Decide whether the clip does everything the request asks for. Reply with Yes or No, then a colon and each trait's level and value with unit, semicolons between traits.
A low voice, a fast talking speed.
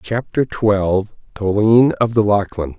No: low, 105 Hz; slow, 130 wpm